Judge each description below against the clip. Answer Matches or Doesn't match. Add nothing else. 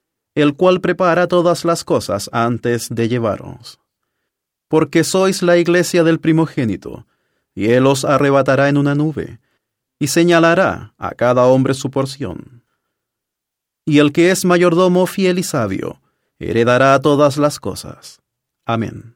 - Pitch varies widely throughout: Matches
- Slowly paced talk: Matches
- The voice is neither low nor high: Matches